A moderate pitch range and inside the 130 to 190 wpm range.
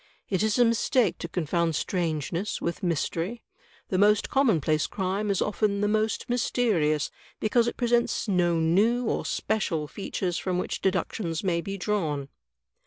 Yes: average, 4.3 semitones; average, 150 wpm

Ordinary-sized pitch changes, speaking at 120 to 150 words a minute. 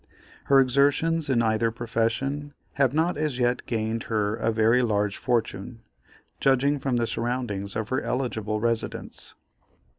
Yes: average, 3.5 semitones; average, 140 wpm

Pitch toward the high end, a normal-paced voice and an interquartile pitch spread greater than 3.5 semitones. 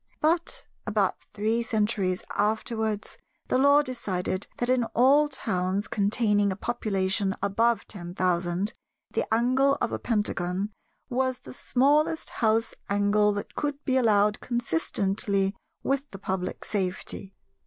No: high, 215 Hz; slow, 125 wpm; average, 4.2 semitones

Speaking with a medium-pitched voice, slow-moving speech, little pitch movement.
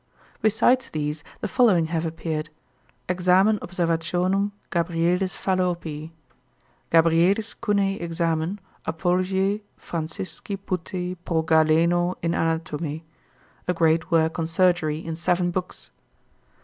Yes: medium, 170 Hz; slow, 100 wpm; narrow, 2.3 semitones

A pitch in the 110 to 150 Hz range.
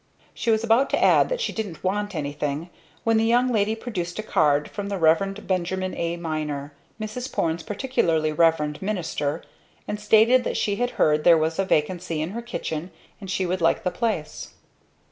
No: medium, 185 Hz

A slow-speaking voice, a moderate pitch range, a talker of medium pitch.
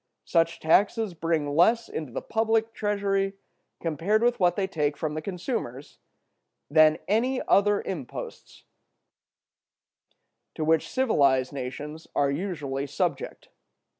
No: slow, 115 wpm; wide, 5.7 semitones; medium, 165 Hz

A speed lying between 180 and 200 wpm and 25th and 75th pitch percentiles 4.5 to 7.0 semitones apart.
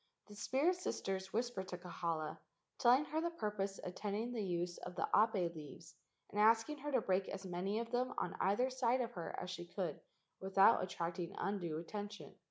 Yes: average, 185 wpm; average, 4.9 semitones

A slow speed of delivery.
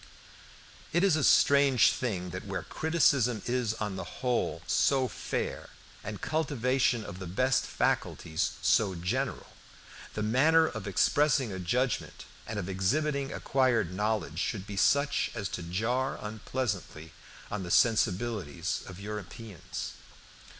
Yes: slow, 130 wpm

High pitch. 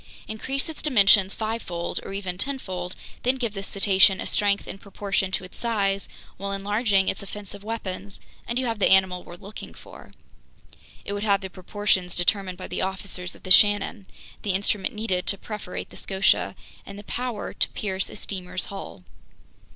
Yes: high, 200 Hz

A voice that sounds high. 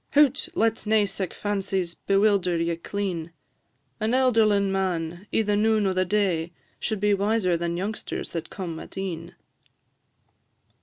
Yes: high, 195 Hz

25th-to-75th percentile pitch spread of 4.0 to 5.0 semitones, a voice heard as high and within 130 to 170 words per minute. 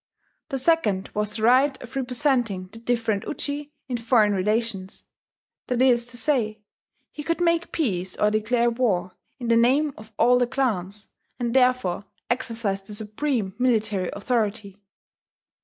No: average, 3.5 semitones; high, 235 Hz; average, 145 wpm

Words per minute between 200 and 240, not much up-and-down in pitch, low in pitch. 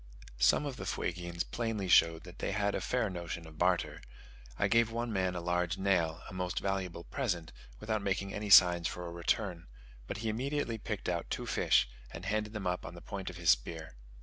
No: fast, 205 wpm; average, 3.5 semitones; very low, 90 Hz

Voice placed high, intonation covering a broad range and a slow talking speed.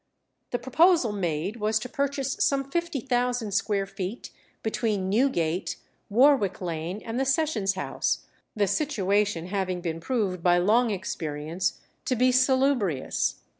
Yes: high, 210 Hz; wide, 5.8 semitones; slow, 130 wpm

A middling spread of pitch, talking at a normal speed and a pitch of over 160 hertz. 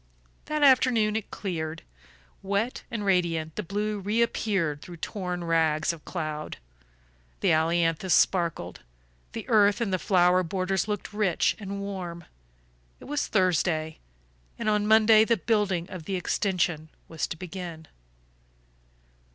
No: average, 4.0 semitones; slow, 130 wpm; medium, 185 Hz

